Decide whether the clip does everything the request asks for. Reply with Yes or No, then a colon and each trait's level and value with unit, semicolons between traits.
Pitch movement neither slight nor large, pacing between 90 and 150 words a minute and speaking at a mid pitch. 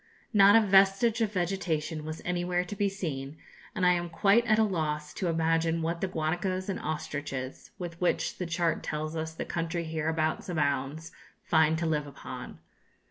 No: average, 3.0 semitones; average, 175 wpm; medium, 165 Hz